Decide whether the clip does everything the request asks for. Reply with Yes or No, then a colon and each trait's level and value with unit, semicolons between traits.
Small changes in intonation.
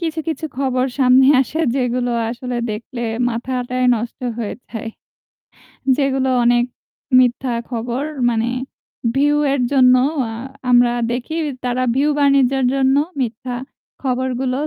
Yes: narrow, 1.7 semitones